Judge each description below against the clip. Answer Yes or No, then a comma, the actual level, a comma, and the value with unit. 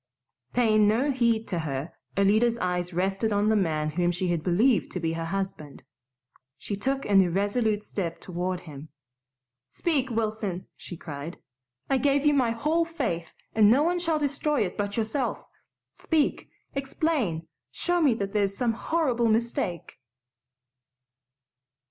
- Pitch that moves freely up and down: Yes, wide, 6.6 semitones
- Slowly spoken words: No, average, 145 wpm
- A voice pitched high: Yes, high, 210 Hz